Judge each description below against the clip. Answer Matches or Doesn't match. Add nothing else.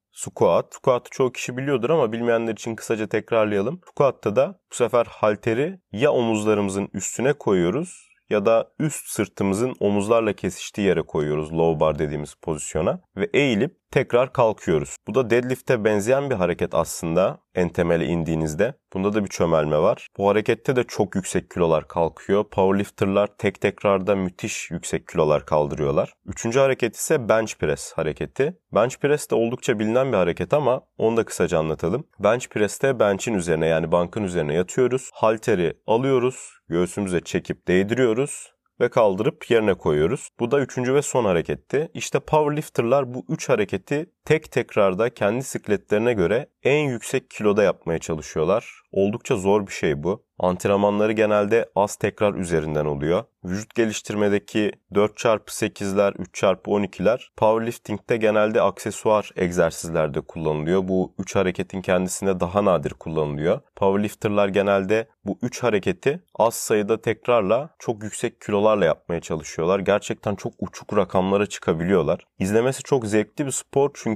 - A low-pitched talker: Matches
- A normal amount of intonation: Matches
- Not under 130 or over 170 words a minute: Matches